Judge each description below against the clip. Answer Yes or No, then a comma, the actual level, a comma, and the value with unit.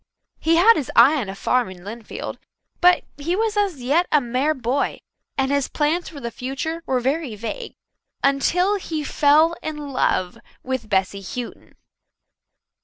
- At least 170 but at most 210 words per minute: No, average, 160 wpm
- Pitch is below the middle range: No, very high, 280 Hz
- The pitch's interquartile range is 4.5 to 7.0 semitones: Yes, average, 5.1 semitones